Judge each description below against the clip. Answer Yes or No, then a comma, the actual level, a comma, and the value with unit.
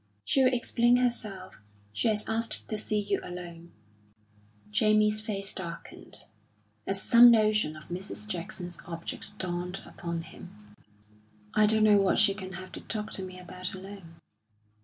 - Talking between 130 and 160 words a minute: Yes, average, 145 wpm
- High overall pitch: Yes, high, 195 Hz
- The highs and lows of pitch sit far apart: No, average, 3.2 semitones